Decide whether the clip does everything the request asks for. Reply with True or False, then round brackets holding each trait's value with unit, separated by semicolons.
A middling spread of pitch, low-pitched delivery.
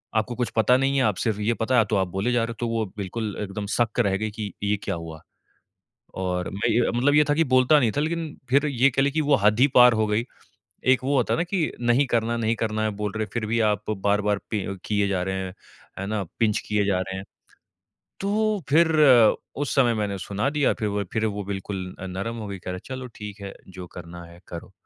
True (4.1 semitones; 110 Hz)